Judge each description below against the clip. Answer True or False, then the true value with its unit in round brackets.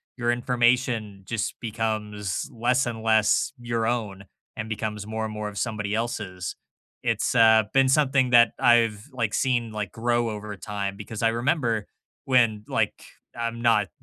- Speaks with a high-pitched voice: False (115 Hz)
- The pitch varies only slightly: True (2.1 semitones)